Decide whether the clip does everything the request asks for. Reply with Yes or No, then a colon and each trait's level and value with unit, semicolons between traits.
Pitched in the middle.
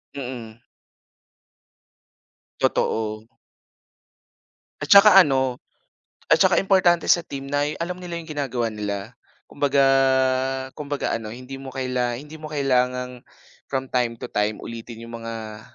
No: low, 130 Hz